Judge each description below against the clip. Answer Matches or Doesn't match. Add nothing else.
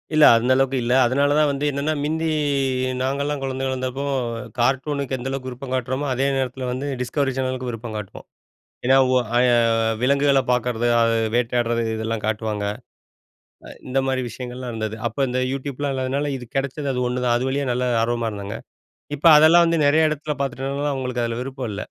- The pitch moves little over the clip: Matches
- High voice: Doesn't match